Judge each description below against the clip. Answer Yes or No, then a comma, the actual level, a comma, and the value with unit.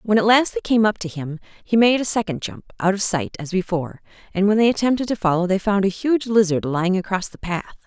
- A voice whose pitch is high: Yes, high, 200 Hz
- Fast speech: Yes, fast, 235 wpm